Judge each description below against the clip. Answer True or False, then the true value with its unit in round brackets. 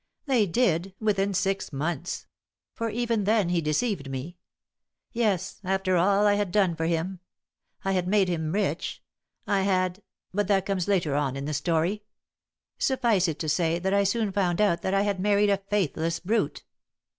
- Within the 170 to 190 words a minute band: True (175 wpm)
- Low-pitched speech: False (190 Hz)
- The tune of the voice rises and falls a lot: False (3.3 semitones)